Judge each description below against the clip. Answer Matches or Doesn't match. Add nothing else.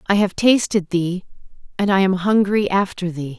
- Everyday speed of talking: Matches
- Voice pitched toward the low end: Doesn't match